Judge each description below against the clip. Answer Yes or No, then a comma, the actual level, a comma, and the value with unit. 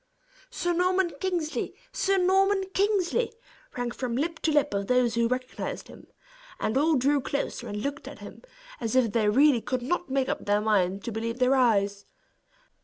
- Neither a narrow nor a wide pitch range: No, wide, 7.1 semitones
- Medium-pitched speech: No, very high, 260 Hz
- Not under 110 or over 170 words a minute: No, average, 180 wpm